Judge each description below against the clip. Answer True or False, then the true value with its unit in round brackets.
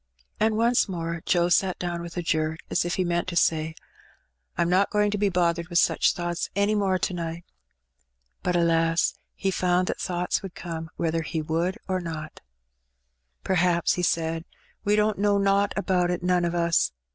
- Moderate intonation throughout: False (2.2 semitones)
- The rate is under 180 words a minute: False (190 wpm)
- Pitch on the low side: False (175 Hz)